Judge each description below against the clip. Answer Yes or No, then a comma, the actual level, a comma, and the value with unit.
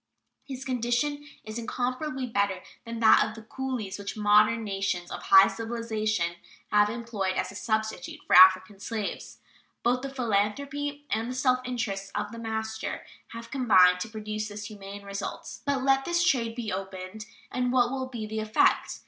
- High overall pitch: Yes, high, 220 Hz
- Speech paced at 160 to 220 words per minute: Yes, average, 165 wpm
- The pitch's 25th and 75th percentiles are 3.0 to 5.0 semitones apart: Yes, average, 3.7 semitones